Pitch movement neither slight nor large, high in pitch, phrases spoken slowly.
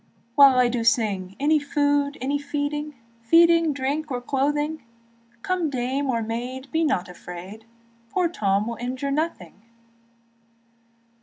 Yes: average, 4.2 semitones; very high, 275 Hz; slow, 130 wpm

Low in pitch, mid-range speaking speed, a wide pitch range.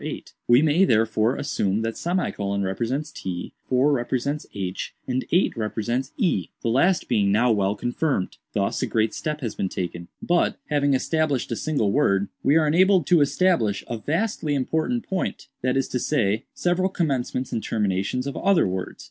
Yes: low, 130 Hz; average, 165 wpm; wide, 6.5 semitones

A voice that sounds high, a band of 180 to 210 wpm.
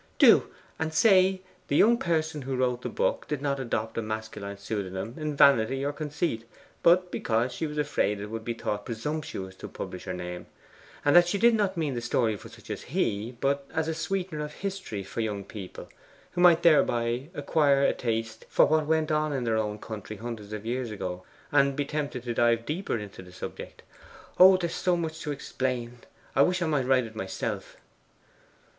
No: low, 135 Hz; average, 200 wpm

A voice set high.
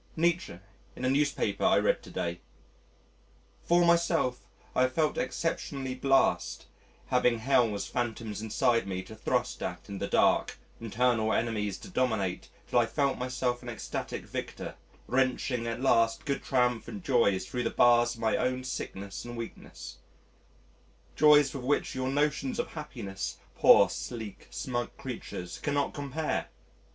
No: low, 125 Hz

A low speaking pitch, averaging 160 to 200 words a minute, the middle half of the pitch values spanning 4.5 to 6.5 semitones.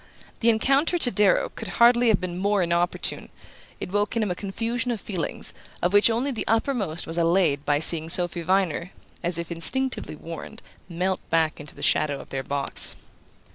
No: medium, 185 Hz; average, 180 wpm; average, 5.2 semitones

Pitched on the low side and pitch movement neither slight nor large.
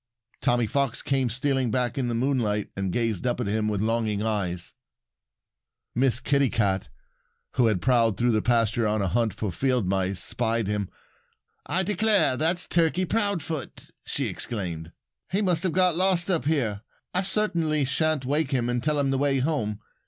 No: low, 125 Hz; wide, 6.3 semitones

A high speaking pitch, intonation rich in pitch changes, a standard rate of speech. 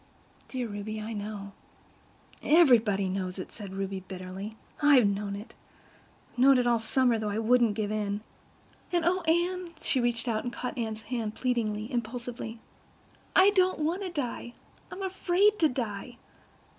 Yes: high, 235 Hz; wide, 5.7 semitones; average, 145 wpm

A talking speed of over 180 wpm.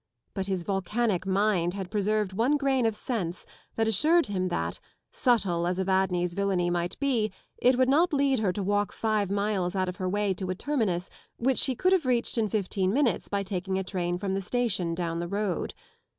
Yes: average, 200 wpm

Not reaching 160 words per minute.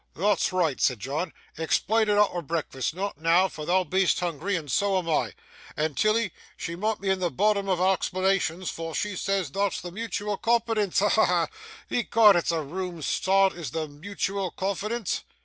No: average, 185 wpm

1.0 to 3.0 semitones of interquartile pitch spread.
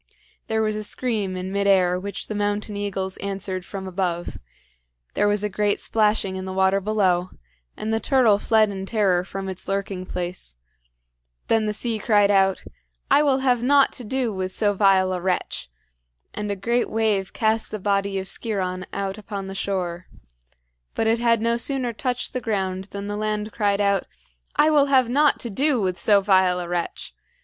Yes: average, 2.7 semitones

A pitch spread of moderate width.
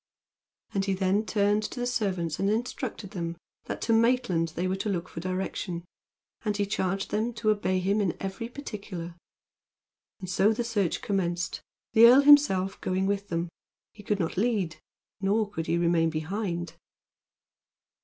Yes: average, 3.4 semitones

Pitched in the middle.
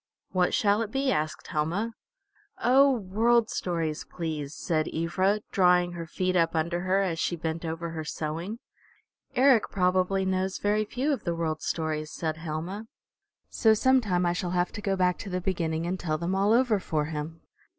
Yes: medium, 180 Hz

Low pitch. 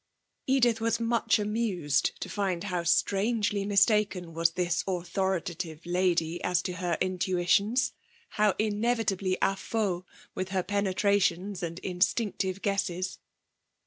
No: high, 190 Hz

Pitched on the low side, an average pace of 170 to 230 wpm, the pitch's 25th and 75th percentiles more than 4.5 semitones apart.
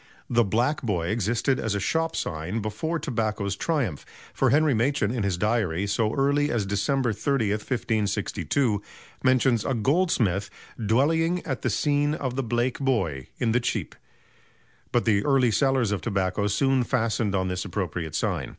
No: low, 115 Hz; average, 160 wpm; average, 4.9 semitones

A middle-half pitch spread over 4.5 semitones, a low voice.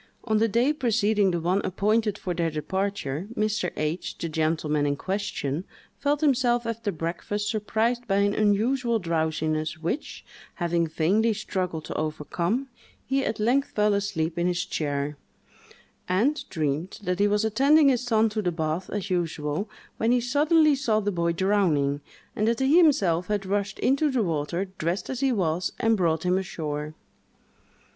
No: wide, 5.5 semitones; high, 200 Hz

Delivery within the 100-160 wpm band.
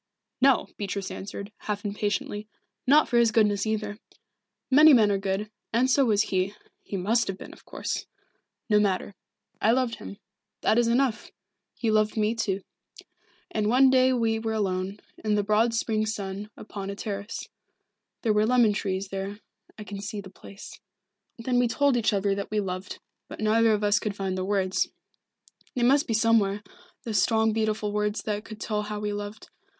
No: average, 180 wpm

